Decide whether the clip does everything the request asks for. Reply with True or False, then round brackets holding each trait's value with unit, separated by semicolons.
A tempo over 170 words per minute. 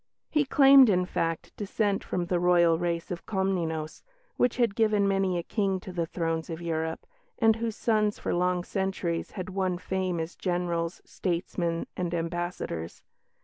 False (160 wpm)